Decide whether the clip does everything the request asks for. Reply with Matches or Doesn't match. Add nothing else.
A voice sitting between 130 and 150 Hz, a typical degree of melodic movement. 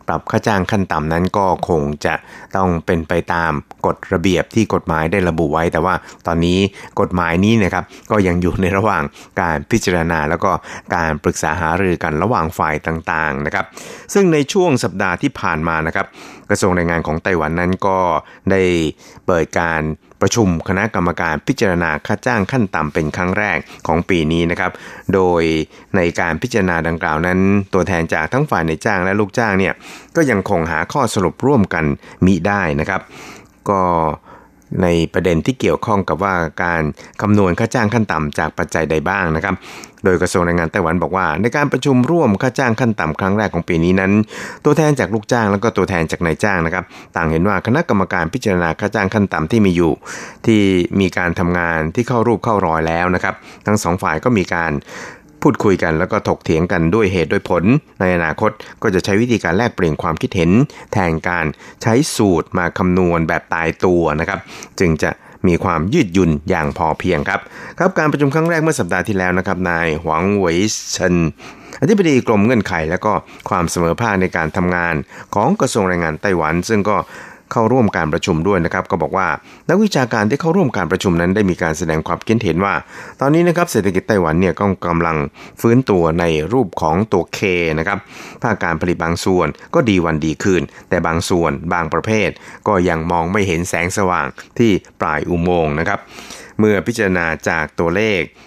Doesn't match